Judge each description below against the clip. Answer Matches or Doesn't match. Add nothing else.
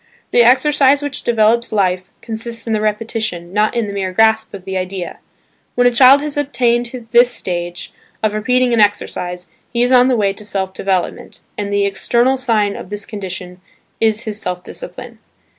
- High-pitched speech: Matches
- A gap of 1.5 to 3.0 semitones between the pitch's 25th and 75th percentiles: Doesn't match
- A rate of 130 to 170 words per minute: Doesn't match